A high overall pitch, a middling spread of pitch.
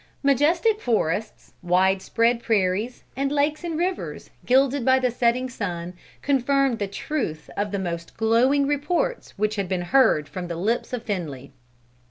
No: high, 235 Hz; wide, 6.5 semitones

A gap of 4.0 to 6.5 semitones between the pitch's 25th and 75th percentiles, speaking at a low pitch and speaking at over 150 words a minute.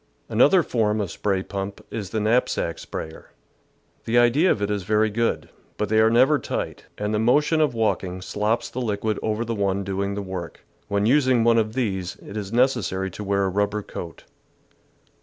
No: average, 3.0 semitones; low, 105 Hz; average, 190 wpm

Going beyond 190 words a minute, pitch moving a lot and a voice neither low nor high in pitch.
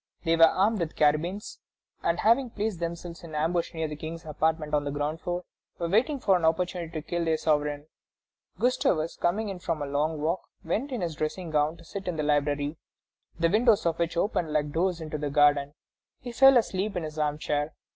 No: average, 200 wpm; average, 3.1 semitones; medium, 165 Hz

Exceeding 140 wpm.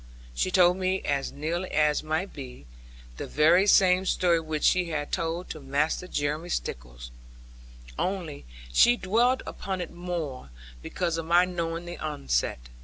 Yes: average, 150 wpm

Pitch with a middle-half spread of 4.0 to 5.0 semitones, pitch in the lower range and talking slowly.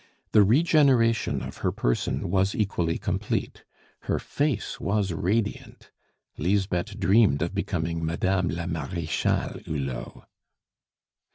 Yes: average, 4.4 semitones; very low, 95 Hz; slow, 105 wpm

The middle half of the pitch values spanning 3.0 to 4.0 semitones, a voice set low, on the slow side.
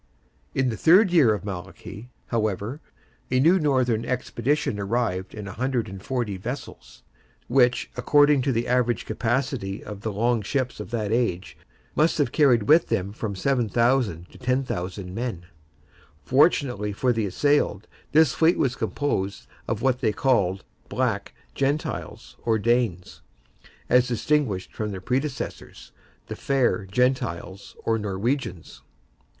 No: average, 4.6 semitones; low, 120 Hz; slow, 130 wpm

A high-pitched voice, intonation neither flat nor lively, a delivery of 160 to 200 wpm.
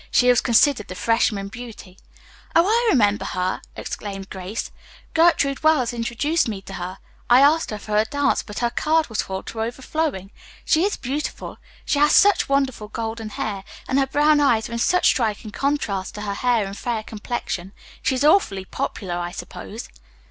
No: high, 235 Hz; wide, 5.8 semitones; average, 175 wpm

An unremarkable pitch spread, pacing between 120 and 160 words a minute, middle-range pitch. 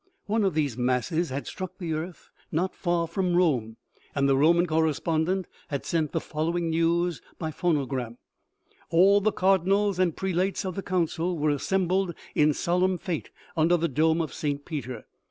No: average, 3.2 semitones; average, 170 wpm; medium, 170 Hz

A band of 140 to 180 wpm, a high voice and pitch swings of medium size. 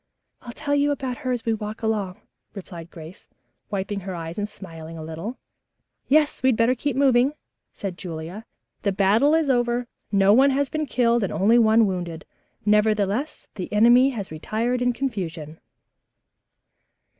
Yes: average, 160 wpm; high, 220 Hz; average, 4.8 semitones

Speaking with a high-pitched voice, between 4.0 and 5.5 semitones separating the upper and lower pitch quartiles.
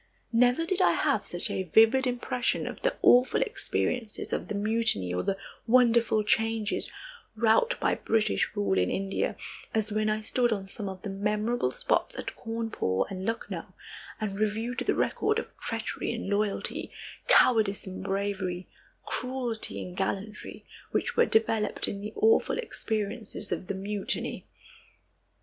No: high, 215 Hz; average, 3.3 semitones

